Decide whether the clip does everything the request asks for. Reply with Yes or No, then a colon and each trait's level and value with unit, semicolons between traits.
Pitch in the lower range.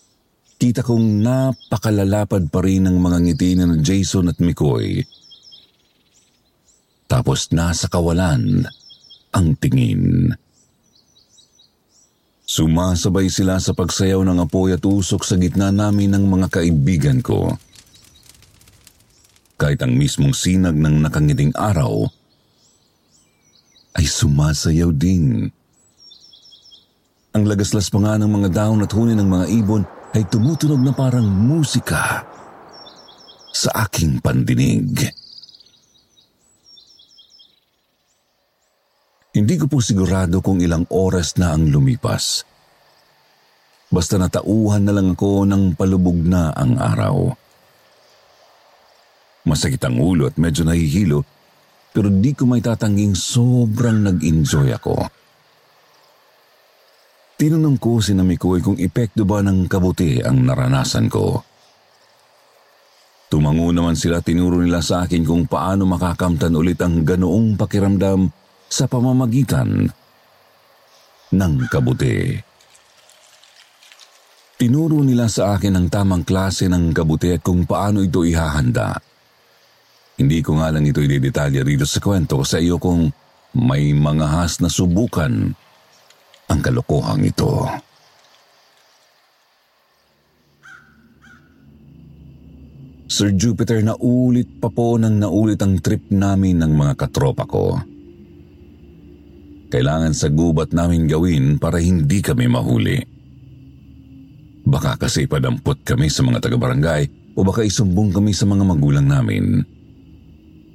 Yes: very low, 95 Hz